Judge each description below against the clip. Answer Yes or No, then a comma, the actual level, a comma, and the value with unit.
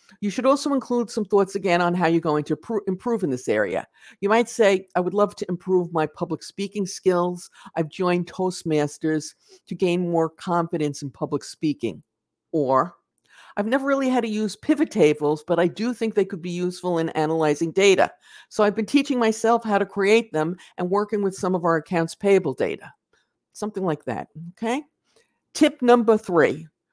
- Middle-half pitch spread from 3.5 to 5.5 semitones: Yes, average, 4.9 semitones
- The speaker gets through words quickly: No, average, 185 wpm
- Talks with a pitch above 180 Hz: Yes, high, 190 Hz